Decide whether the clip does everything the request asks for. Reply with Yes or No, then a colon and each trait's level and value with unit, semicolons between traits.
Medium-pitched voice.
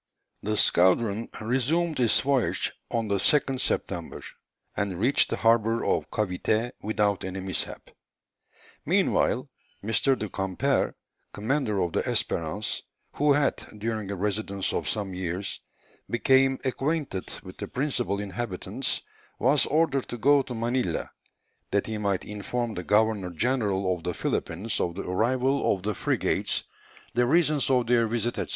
No: low, 110 Hz